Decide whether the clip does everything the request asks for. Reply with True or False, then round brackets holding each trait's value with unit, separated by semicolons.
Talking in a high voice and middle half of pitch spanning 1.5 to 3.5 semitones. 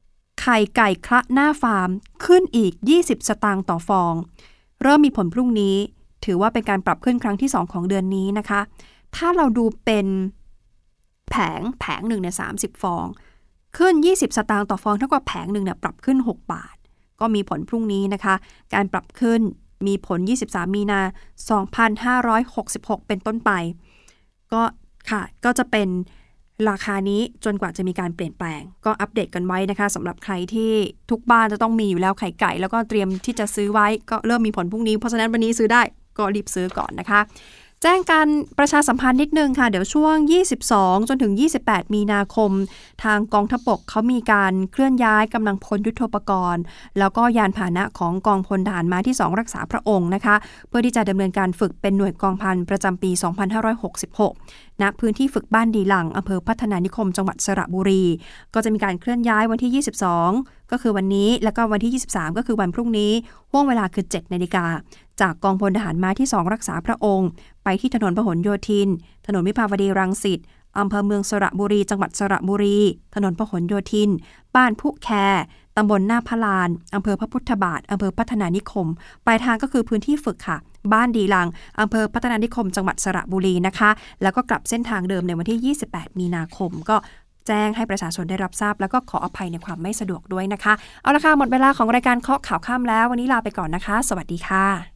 True (210 Hz; 3.2 semitones)